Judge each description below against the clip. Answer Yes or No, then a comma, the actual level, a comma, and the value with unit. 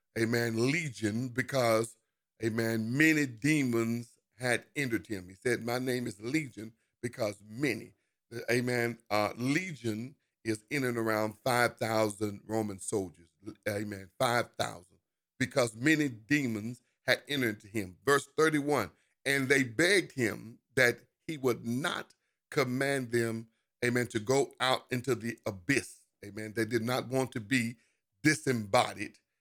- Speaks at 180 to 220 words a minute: No, slow, 135 wpm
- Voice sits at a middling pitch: No, low, 120 Hz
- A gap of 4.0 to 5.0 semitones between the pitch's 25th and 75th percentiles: No, average, 3.1 semitones